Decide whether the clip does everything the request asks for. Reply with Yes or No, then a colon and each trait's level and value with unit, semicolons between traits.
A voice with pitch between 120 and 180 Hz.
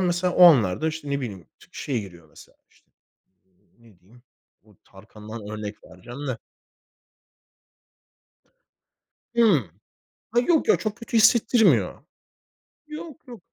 Yes: medium, 140 Hz